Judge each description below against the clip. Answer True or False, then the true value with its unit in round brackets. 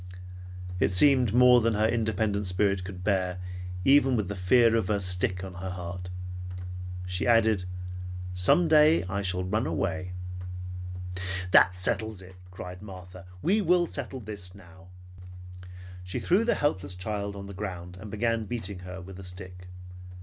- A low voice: True (100 Hz)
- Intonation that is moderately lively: True (3.7 semitones)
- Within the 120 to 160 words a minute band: True (155 wpm)